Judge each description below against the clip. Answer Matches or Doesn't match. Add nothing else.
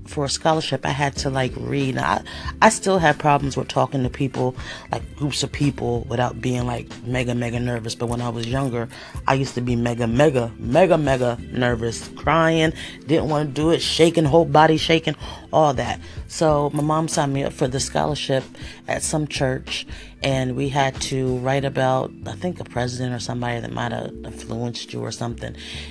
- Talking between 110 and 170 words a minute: Doesn't match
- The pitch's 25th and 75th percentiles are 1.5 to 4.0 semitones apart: Matches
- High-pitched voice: Doesn't match